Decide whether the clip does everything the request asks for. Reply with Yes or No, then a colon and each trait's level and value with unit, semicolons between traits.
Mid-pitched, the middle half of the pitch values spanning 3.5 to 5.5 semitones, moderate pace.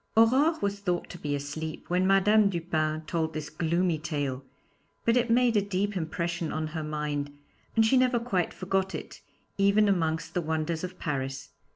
Yes: medium, 175 Hz; average, 4.4 semitones; average, 175 wpm